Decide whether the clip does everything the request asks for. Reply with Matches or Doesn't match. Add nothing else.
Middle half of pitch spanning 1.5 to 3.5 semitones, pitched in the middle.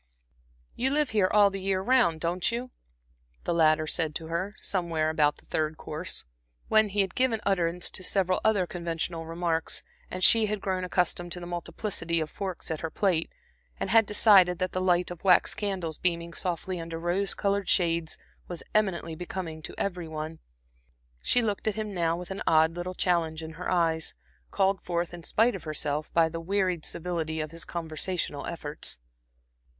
Matches